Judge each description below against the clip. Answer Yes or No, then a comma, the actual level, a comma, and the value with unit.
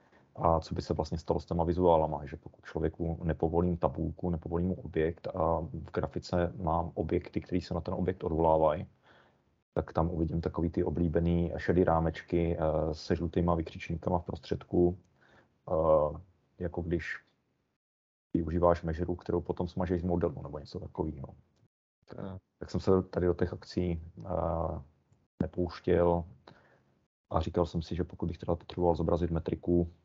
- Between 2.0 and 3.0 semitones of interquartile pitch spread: No, narrow, 1.5 semitones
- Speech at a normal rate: Yes, average, 140 wpm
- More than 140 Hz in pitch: No, very low, 85 Hz